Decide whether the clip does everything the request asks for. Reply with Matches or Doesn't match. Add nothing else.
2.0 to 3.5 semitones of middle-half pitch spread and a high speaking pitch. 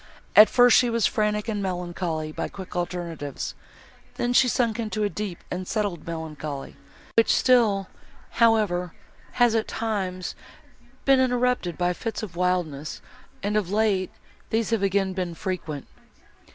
Doesn't match